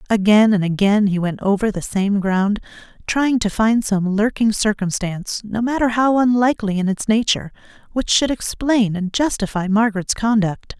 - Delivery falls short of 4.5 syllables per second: No, 5.0 syllables/s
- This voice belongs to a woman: Yes, female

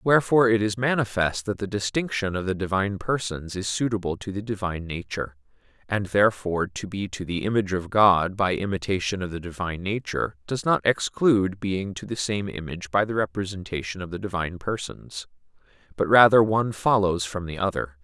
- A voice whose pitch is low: Yes, low, 100 Hz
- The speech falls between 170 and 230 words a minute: Yes, average, 180 wpm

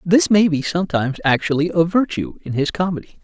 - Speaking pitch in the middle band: Yes, medium, 170 Hz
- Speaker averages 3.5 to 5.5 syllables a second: No, 5.9 syllables/s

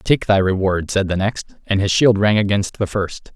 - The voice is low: Yes, low, 100 Hz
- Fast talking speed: Yes, fast, 235 wpm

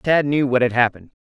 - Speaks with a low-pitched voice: Yes, low, 130 Hz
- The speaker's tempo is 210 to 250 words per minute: Yes, fast, 240 wpm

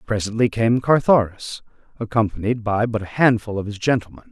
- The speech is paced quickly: No, average, 155 wpm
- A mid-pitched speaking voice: No, low, 110 Hz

